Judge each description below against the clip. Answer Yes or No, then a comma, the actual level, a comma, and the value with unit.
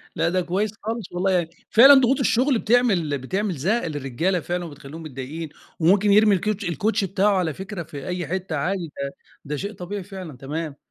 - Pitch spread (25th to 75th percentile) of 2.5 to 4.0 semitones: No, average, 4.6 semitones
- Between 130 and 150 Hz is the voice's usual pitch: No, medium, 180 Hz